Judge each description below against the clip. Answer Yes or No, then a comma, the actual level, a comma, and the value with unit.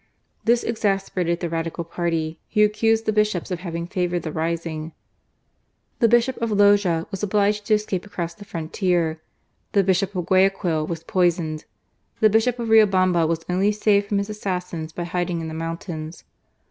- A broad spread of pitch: No, average, 3.8 semitones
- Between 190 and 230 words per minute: No, average, 165 wpm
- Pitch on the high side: No, medium, 180 Hz